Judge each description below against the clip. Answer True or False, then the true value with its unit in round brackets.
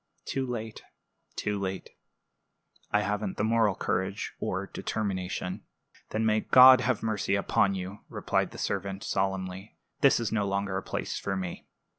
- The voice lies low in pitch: True (100 Hz)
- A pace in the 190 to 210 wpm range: False (150 wpm)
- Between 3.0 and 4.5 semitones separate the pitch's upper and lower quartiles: False (2.4 semitones)